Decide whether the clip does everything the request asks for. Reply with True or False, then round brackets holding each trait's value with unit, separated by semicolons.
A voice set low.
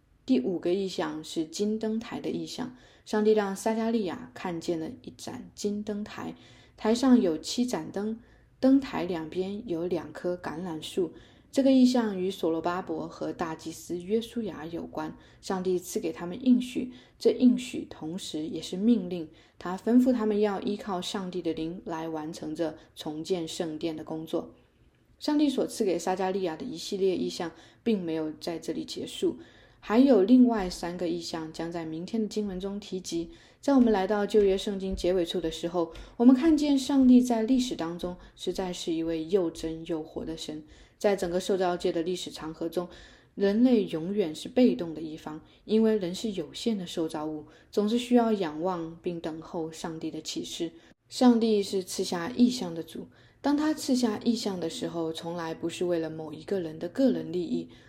False (180 Hz)